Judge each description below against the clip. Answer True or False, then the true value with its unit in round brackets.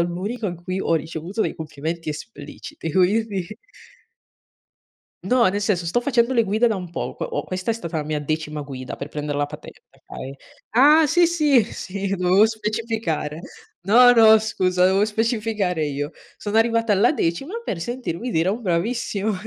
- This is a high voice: True (195 Hz)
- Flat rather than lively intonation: False (5.5 semitones)